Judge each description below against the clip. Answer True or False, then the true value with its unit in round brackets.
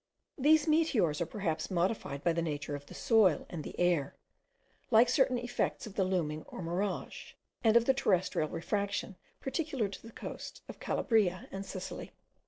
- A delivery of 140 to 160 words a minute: False (170 wpm)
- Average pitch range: False (5.8 semitones)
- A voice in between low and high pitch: False (195 Hz)